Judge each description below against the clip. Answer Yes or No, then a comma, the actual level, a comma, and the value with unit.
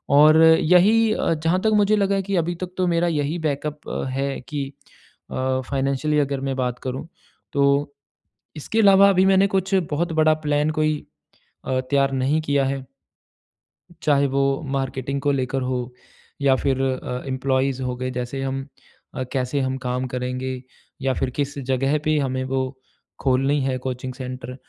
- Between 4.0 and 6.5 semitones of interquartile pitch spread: No, average, 3.1 semitones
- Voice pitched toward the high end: No, medium, 140 Hz